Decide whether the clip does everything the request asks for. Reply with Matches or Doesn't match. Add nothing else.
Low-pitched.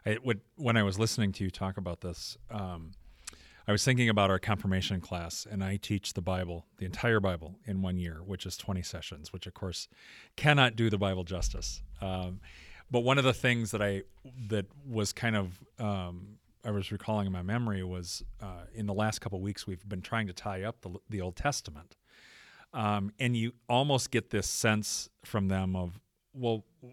Matches